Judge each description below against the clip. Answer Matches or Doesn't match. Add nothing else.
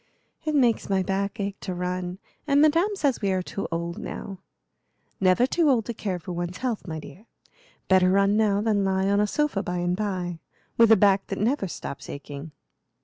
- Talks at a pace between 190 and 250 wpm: Matches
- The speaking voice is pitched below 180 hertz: Doesn't match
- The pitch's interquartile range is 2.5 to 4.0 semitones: Matches